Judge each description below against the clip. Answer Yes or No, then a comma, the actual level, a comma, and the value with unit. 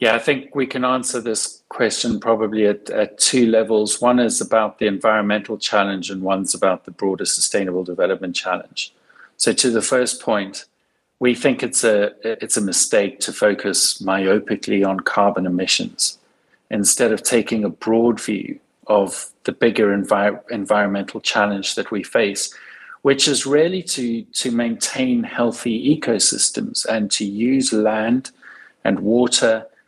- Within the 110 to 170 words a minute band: Yes, average, 150 wpm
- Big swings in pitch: No, average, 3.2 semitones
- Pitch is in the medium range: No, low, 110 Hz